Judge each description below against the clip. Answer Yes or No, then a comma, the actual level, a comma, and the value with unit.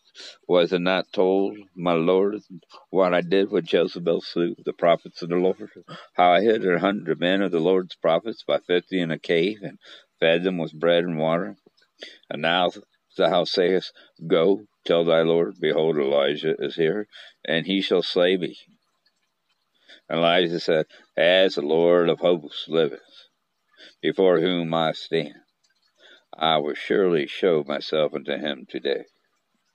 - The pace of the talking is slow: No, average, 155 wpm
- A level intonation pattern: Yes, narrow, 2.1 semitones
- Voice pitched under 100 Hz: Yes, very low, 90 Hz